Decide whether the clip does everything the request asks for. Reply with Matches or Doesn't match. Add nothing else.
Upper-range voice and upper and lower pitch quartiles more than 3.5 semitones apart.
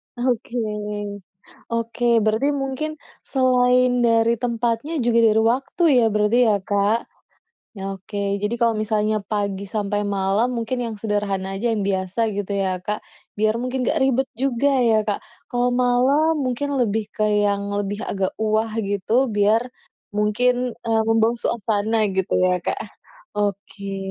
Doesn't match